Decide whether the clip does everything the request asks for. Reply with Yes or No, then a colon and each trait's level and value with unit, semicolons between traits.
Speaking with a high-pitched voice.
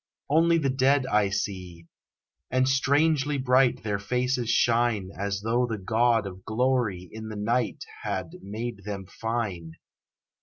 No: low, 115 Hz